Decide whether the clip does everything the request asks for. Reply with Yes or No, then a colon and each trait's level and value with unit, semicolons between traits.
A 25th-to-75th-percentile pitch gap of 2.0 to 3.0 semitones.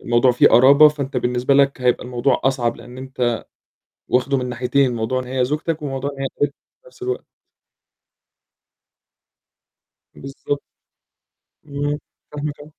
Yes: narrow, 2.5 semitones